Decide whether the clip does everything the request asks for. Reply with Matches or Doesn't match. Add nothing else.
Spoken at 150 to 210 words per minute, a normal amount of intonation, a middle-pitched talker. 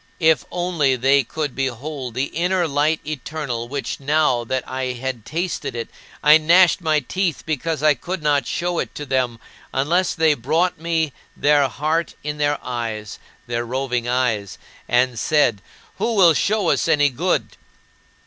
Matches